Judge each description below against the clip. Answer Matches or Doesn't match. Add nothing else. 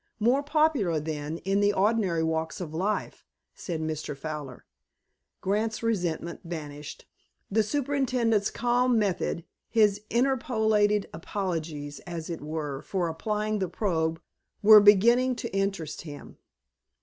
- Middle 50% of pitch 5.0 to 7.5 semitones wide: Matches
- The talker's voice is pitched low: Doesn't match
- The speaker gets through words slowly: Matches